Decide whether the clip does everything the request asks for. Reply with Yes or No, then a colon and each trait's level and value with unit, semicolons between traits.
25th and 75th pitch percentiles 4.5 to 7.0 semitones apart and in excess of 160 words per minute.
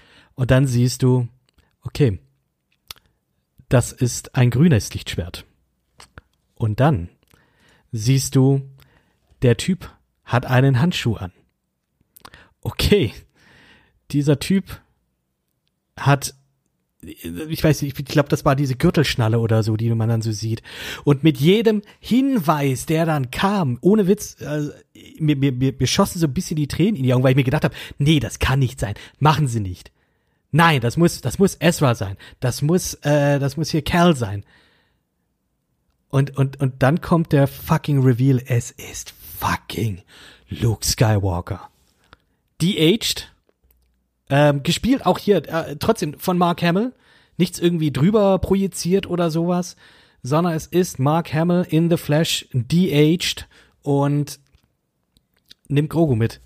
No: wide, 5.4 semitones; average, 140 wpm